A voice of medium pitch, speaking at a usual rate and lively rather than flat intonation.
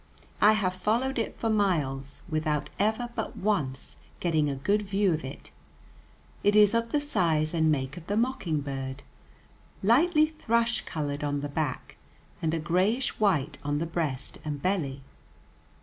Yes: medium, 170 Hz; average, 155 wpm; wide, 6.7 semitones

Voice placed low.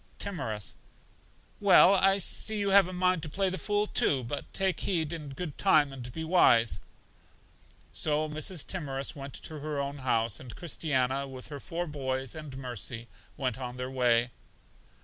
No: medium, 145 Hz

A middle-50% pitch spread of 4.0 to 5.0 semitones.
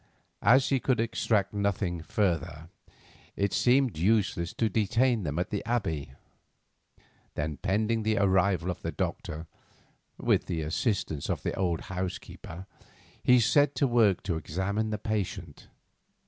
Yes: average, 4.6 semitones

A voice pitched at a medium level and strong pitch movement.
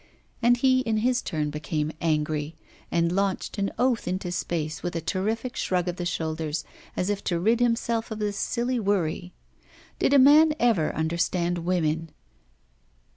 Yes: medium, 180 Hz; wide, 5.8 semitones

